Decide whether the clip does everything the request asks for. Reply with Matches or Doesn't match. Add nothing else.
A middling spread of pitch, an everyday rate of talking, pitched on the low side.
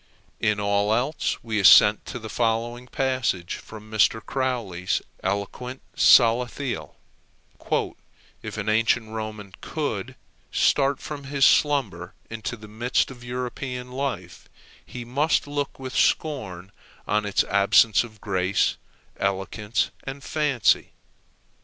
Doesn't match